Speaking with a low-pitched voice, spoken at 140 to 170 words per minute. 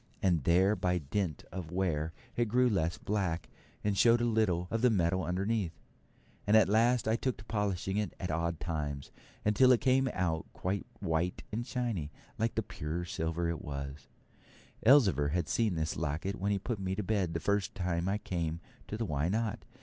No: very low, 95 Hz; average, 195 wpm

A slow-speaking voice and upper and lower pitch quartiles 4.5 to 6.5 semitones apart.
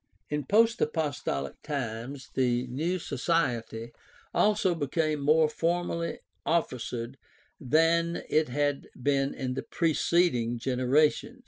Yes: slow, 110 wpm; average, 4.8 semitones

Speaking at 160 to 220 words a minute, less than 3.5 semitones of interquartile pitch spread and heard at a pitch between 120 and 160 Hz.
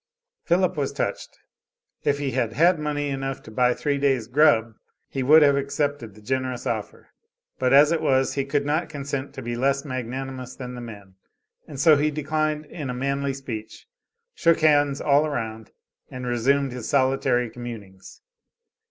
Yes: average, 170 wpm; average, 2.9 semitones; low, 135 Hz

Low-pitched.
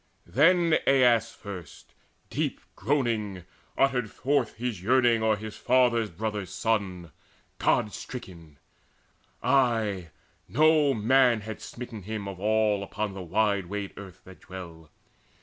Yes: low, 110 Hz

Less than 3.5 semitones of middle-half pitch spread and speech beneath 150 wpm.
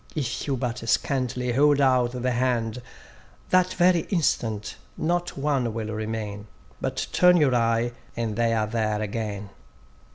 No: average, 4.0 semitones; average, 140 wpm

